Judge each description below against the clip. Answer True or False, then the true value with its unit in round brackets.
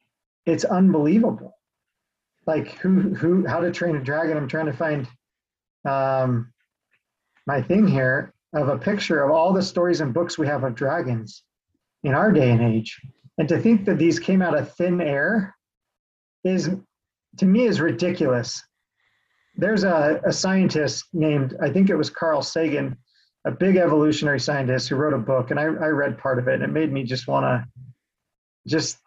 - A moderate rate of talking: True (175 wpm)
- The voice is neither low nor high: True (155 Hz)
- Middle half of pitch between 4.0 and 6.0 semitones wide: True (4.6 semitones)